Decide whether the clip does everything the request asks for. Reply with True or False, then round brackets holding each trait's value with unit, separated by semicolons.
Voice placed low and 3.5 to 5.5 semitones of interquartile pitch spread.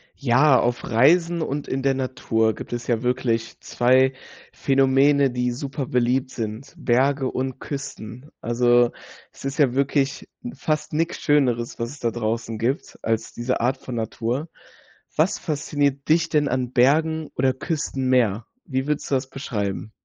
False (130 Hz; 2.8 semitones)